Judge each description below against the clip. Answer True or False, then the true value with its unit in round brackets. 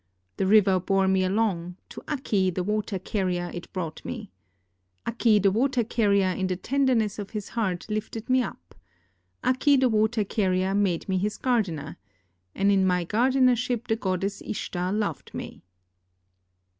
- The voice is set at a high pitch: True (205 Hz)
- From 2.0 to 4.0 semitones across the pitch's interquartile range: True (3.5 semitones)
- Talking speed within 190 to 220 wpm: False (155 wpm)